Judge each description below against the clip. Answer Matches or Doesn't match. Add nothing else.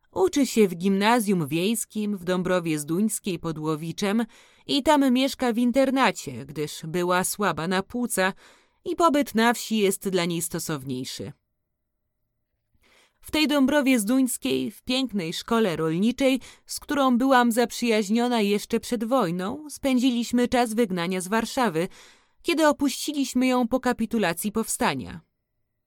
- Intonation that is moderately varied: Doesn't match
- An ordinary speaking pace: Matches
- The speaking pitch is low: Doesn't match